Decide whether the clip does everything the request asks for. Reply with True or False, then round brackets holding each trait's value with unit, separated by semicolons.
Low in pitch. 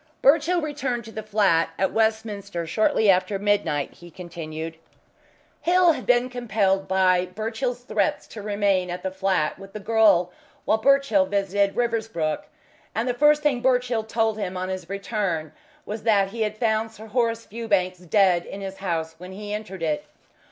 False (205 Hz)